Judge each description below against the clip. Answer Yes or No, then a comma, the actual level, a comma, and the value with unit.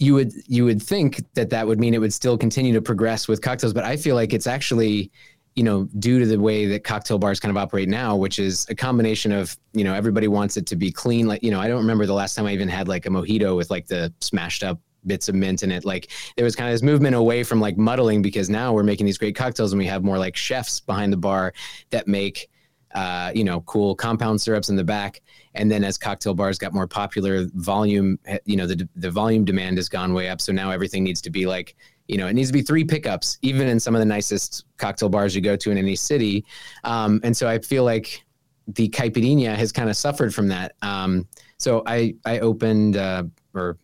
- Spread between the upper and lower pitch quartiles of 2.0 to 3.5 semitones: Yes, average, 2.9 semitones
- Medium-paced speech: No, fast, 245 wpm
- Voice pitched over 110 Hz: No, low, 105 Hz